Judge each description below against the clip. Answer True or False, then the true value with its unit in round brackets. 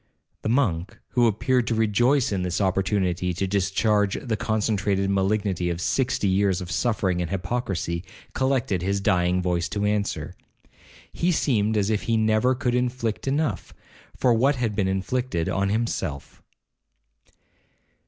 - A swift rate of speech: False (145 wpm)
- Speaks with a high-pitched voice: False (105 Hz)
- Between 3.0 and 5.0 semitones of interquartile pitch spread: True (4.0 semitones)